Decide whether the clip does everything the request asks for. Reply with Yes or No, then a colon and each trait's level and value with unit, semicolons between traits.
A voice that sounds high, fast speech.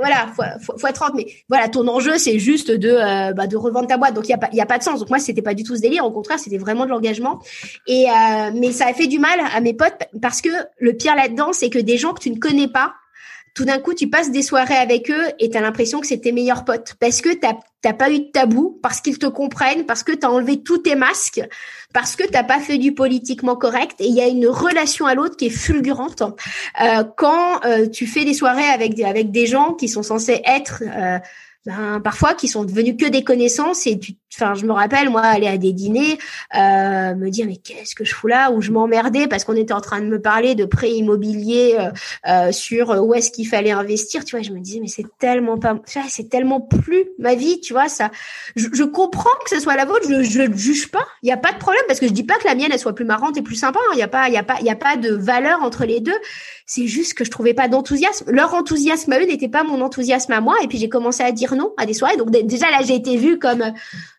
Yes: very high, 250 Hz; fast, 275 wpm